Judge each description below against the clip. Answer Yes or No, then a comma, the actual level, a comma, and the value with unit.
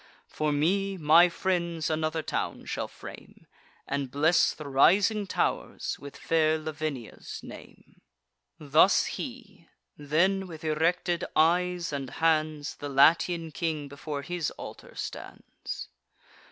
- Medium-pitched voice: Yes, medium, 160 Hz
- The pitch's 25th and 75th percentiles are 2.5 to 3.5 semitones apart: Yes, average, 2.9 semitones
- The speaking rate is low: Yes, slow, 115 wpm